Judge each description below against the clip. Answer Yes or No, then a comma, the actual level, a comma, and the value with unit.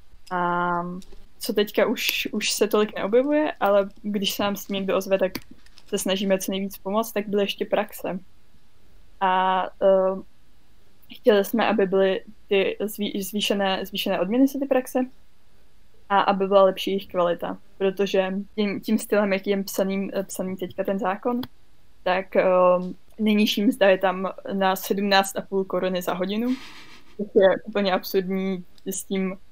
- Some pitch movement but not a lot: No, narrow, 1.8 semitones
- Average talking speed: Yes, average, 145 wpm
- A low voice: No, high, 195 Hz